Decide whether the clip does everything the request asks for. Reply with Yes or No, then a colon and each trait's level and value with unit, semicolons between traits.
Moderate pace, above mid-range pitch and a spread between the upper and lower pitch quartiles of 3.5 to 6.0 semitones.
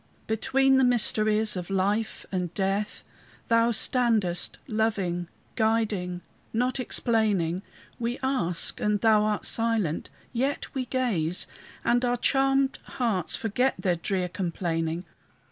No: slow, 115 wpm; high, 215 Hz; average, 4.8 semitones